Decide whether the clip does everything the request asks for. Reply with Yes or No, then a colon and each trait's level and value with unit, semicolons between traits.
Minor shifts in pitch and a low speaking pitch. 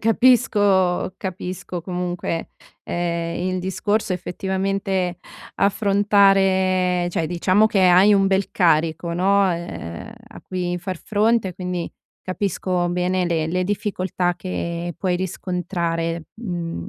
No: narrow, 1.9 semitones; medium, 185 Hz